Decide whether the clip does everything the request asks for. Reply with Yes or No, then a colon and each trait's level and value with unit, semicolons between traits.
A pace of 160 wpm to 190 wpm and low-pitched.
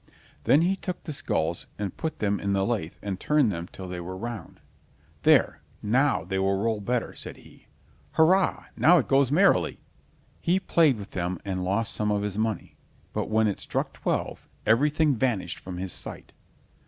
Yes: average, 180 wpm; low, 110 Hz